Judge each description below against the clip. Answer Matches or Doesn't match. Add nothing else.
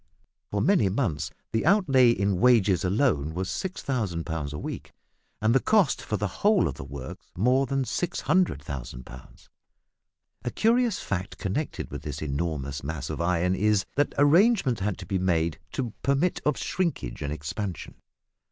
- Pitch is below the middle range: Matches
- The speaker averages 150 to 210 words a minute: Matches